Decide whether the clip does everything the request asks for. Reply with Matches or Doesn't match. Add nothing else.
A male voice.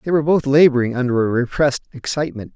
Matches